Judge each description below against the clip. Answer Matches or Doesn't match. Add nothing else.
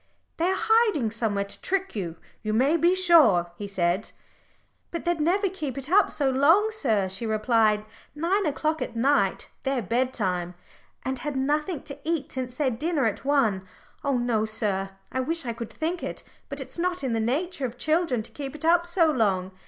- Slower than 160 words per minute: Doesn't match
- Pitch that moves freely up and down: Matches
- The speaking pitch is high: Matches